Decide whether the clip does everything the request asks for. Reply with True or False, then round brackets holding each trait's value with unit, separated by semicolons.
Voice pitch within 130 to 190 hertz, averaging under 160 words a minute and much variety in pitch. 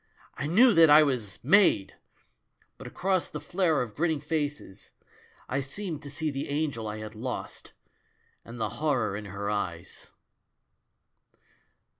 True (140 Hz; 140 wpm; 6.4 semitones)